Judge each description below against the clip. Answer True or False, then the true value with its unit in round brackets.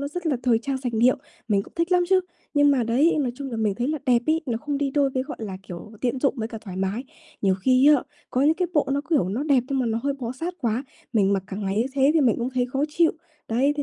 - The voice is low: False (255 Hz)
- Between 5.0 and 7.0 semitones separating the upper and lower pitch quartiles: False (4.2 semitones)